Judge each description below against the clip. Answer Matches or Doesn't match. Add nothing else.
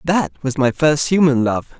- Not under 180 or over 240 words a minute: Matches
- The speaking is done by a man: Matches